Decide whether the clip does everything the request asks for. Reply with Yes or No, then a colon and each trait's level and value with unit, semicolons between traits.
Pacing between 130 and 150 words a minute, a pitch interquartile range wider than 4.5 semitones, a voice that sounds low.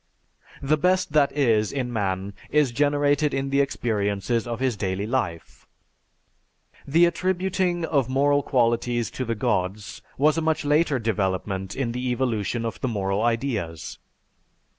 Yes: average, 145 wpm; average, 5.2 semitones; low, 125 Hz